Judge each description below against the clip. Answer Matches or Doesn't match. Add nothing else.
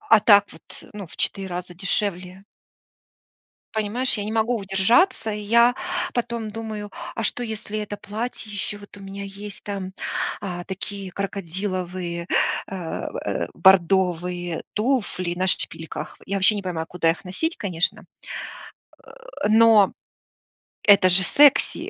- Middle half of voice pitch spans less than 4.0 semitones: Matches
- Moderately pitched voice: Doesn't match